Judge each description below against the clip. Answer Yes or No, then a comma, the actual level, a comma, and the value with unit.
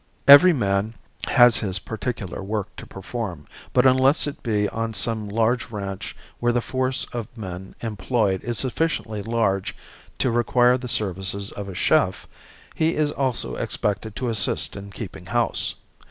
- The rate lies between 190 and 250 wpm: No, average, 155 wpm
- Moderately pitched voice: No, low, 115 Hz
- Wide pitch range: No, average, 3.8 semitones